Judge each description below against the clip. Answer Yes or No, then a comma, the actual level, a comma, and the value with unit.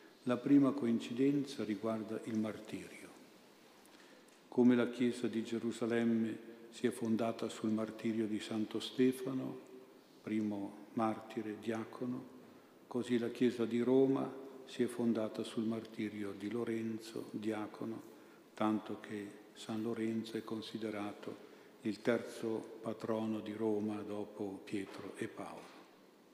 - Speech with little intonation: Yes, narrow, 1.5 semitones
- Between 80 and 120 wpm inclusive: Yes, slow, 115 wpm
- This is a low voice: Yes, low, 110 Hz